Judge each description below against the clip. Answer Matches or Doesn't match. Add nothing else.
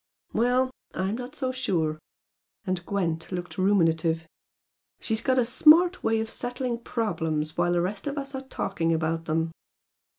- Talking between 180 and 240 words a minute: Doesn't match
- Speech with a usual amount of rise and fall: Doesn't match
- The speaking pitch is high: Matches